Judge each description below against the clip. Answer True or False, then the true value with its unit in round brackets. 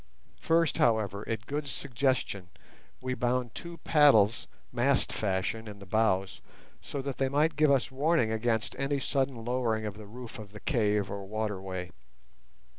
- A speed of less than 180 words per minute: True (155 wpm)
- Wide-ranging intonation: False (4.6 semitones)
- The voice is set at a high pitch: False (115 Hz)